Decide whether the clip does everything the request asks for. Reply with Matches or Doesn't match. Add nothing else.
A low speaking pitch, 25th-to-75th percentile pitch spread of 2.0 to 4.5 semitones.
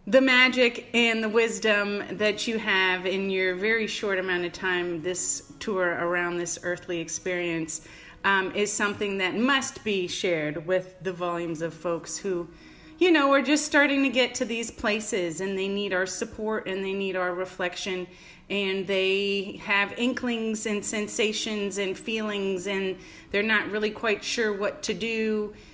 Doesn't match